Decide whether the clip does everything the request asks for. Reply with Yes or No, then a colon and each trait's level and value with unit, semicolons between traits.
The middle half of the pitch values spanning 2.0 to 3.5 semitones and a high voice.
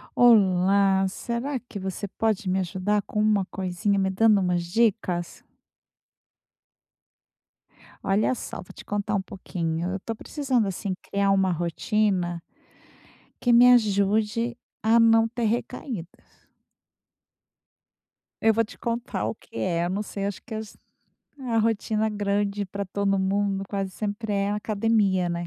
Yes: average, 2.7 semitones; high, 200 Hz